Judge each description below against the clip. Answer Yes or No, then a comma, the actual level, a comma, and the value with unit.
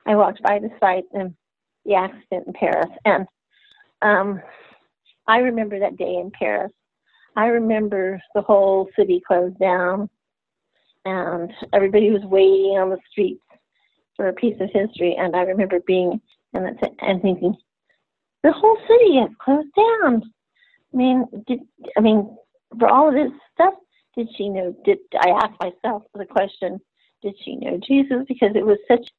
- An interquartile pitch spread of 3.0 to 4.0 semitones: No, average, 4.8 semitones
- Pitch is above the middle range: Yes, high, 210 Hz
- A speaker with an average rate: Yes, average, 160 wpm